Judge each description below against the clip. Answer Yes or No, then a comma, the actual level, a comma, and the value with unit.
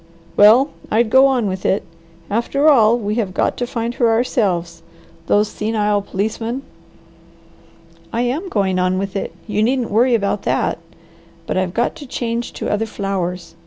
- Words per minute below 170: Yes, average, 160 wpm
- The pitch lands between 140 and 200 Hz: No, high, 220 Hz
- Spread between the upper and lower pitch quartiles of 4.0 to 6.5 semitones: No, average, 3.3 semitones